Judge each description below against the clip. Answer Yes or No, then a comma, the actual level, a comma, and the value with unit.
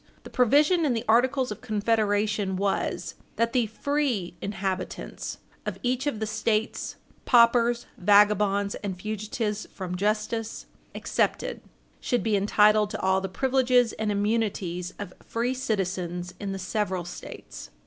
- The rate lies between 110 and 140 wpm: Yes, slow, 135 wpm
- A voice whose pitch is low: No, high, 210 Hz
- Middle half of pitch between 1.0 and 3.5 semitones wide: Yes, average, 3.2 semitones